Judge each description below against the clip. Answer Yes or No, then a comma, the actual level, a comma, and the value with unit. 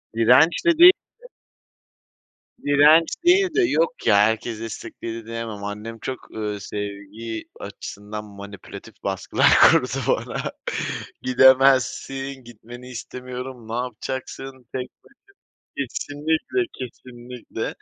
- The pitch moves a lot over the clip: No, average, 3.4 semitones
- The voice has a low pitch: Yes, low, 125 Hz